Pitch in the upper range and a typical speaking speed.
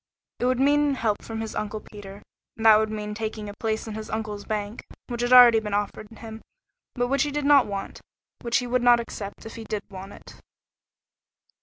No: high, 220 Hz; fast, 210 wpm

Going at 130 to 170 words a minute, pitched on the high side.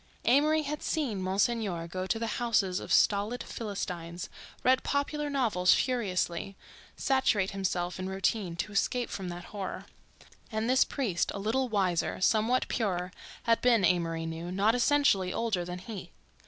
Yes: average, 150 wpm; high, 200 Hz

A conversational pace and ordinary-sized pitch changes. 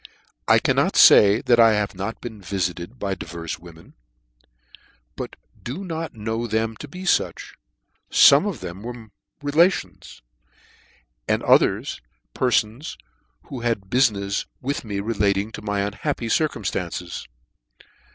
No: slow, 130 wpm; average, 4.0 semitones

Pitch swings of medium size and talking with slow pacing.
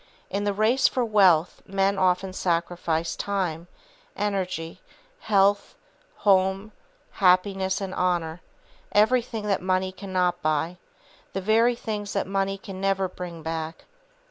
No: narrow, 2.2 semitones; slow, 120 wpm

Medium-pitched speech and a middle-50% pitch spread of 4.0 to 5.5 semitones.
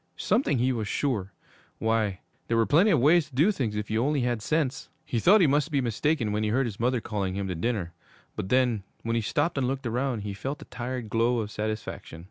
No: low, 120 Hz; average, 4.3 semitones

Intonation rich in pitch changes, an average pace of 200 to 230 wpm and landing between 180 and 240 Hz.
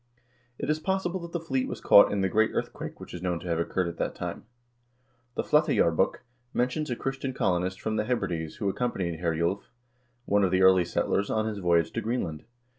No: wide, 6.3 semitones; fast, 205 wpm; low, 100 Hz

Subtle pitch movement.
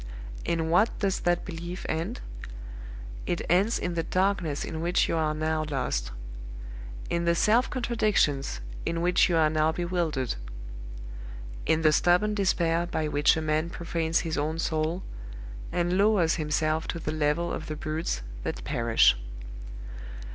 Yes: narrow, 2.2 semitones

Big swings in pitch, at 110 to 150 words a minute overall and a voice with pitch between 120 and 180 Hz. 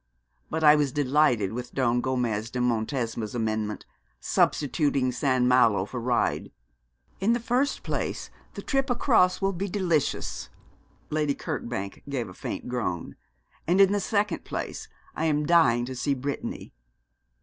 Yes: wide, 5.9 semitones; average, 145 wpm; low, 135 Hz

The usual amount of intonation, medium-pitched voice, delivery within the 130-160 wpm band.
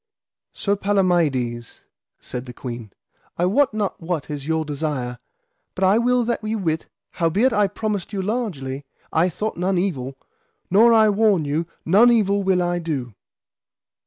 No: wide, 6.0 semitones; medium, 180 Hz; average, 155 wpm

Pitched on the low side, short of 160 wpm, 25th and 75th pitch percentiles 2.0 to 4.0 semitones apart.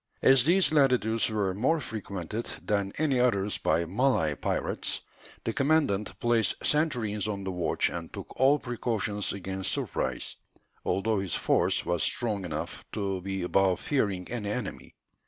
No: low, 105 Hz; average, 145 wpm; average, 4.4 semitones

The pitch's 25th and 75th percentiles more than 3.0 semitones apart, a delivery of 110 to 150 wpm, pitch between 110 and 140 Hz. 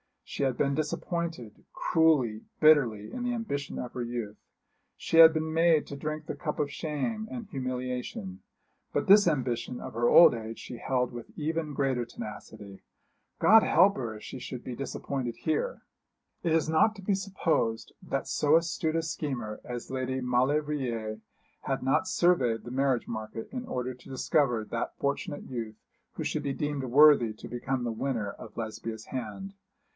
No: average, 4.9 semitones; average, 170 wpm; low, 135 Hz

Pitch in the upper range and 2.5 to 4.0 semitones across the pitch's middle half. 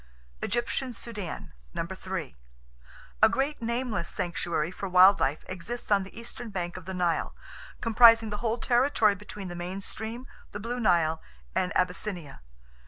No: high, 200 Hz; average, 4.6 semitones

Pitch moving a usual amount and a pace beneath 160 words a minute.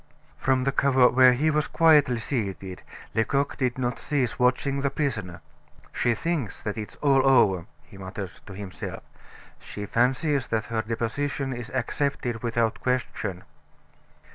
Yes: average, 3.9 semitones; average, 140 wpm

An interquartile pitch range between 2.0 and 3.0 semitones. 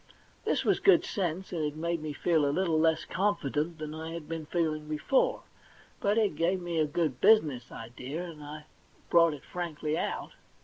Yes: narrow, 2.4 semitones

